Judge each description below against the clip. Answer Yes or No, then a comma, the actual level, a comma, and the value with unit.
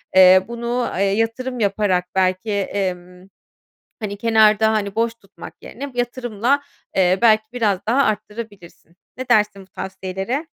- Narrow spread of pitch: No, average, 3.5 semitones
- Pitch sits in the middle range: No, high, 210 Hz